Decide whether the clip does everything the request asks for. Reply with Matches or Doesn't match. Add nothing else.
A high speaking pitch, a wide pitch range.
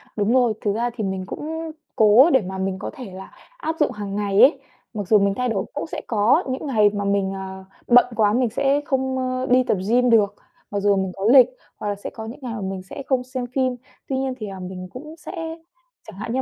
Doesn't match